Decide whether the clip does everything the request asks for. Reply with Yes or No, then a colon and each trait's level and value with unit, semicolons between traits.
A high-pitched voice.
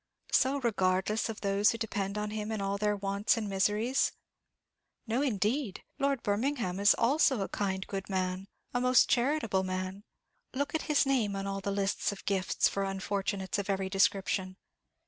Yes: high, 200 Hz